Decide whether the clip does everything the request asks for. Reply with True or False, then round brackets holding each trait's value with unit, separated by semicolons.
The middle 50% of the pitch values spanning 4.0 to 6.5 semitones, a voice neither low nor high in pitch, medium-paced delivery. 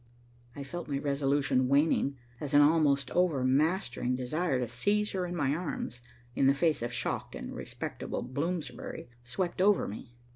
True (4.9 semitones; 145 Hz; 155 wpm)